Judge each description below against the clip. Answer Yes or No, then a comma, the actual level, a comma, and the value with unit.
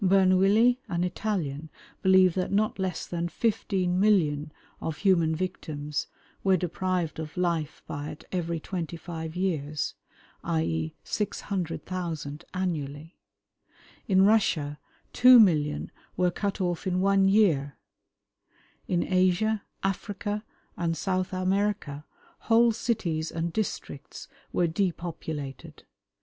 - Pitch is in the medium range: Yes, medium, 180 Hz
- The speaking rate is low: Yes, slow, 110 wpm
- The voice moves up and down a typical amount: Yes, average, 3.5 semitones